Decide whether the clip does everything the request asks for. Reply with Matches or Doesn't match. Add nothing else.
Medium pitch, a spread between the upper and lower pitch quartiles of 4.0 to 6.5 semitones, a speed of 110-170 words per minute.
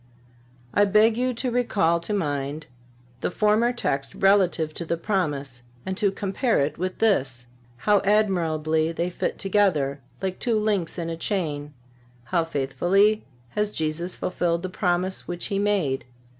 Matches